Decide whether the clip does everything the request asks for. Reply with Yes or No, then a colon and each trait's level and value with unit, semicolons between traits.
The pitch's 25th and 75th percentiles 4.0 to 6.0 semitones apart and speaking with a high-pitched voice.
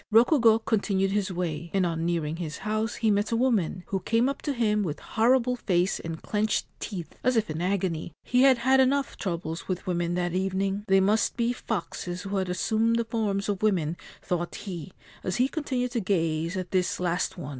Yes: average, 4.5 semitones; high, 195 Hz